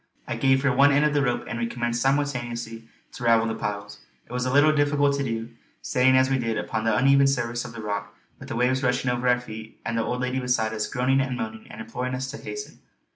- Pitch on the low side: Yes, low, 125 Hz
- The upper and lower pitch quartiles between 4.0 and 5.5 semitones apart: No, average, 2.7 semitones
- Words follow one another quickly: Yes, fast, 250 wpm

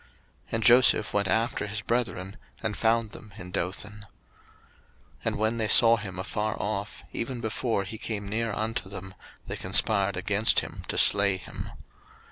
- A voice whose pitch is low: Yes, low, 105 Hz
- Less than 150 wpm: No, average, 160 wpm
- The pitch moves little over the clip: Yes, narrow, 2.3 semitones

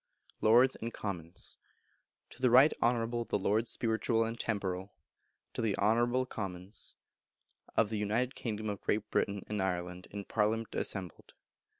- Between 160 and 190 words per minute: No, average, 150 wpm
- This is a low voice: Yes, low, 110 Hz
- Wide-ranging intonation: No, average, 2.8 semitones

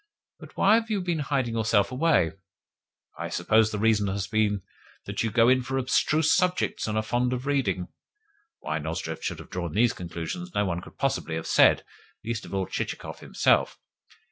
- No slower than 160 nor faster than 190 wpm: Yes, average, 185 wpm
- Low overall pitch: Yes, low, 110 Hz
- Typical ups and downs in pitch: No, wide, 5.7 semitones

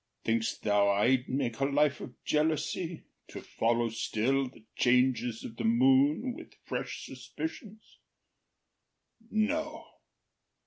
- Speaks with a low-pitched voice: Yes, low, 130 Hz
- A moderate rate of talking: No, slow, 110 wpm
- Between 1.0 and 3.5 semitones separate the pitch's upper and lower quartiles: No, average, 5.1 semitones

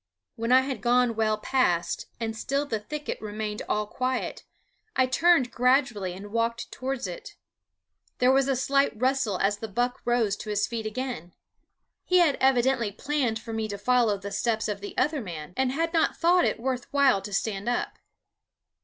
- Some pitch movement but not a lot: Yes, average, 3.9 semitones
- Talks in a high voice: Yes, high, 240 Hz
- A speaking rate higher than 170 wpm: Yes, average, 180 wpm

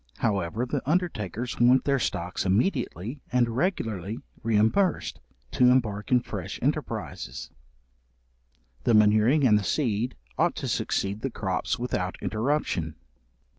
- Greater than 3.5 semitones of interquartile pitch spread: Yes, average, 4.1 semitones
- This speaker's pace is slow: Yes, slow, 120 wpm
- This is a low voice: Yes, low, 115 Hz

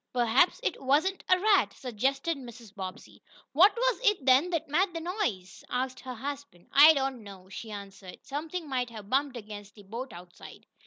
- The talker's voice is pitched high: Yes, very high, 260 Hz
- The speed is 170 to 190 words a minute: Yes, average, 175 wpm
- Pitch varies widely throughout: Yes, wide, 7.0 semitones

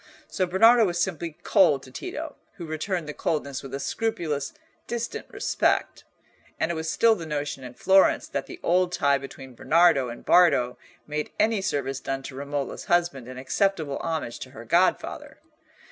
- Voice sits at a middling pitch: Yes, medium, 160 Hz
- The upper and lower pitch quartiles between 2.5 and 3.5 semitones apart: No, wide, 5.4 semitones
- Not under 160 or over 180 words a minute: Yes, average, 170 wpm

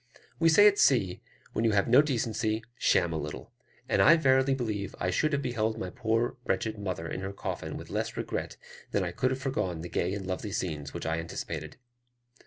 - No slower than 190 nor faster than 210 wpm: Yes, average, 200 wpm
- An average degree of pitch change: No, wide, 6.4 semitones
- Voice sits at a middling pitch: No, low, 110 Hz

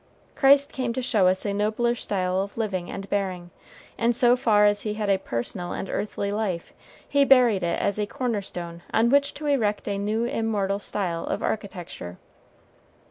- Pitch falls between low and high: No, high, 205 Hz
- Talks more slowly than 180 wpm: No, average, 185 wpm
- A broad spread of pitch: No, average, 3.7 semitones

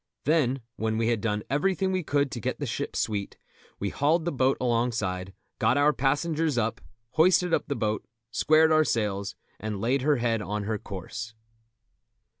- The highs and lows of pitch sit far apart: Yes, wide, 5.8 semitones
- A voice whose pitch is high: No, low, 120 Hz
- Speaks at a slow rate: No, average, 175 wpm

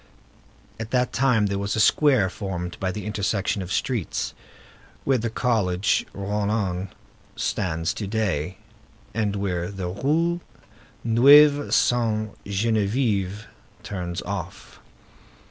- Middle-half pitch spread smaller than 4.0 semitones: Yes, average, 3.4 semitones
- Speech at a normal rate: No, slow, 110 wpm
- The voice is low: Yes, low, 105 Hz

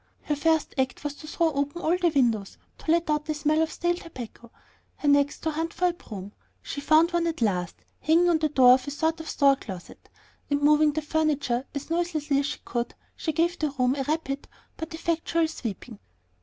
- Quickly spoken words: Yes, fast, 210 wpm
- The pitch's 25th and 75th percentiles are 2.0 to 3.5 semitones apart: Yes, average, 3.0 semitones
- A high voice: Yes, very high, 300 Hz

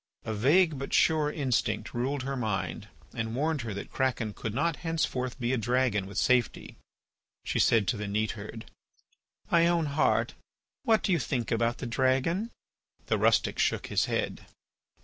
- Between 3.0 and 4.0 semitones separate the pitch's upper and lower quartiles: No, average, 4.8 semitones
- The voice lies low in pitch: Yes, low, 130 Hz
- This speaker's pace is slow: No, average, 165 wpm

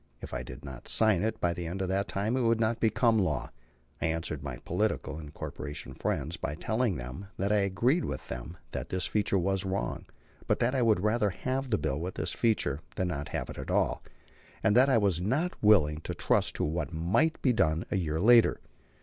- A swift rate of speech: Yes, fast, 225 wpm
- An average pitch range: No, wide, 5.7 semitones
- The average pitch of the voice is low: Yes, very low, 95 Hz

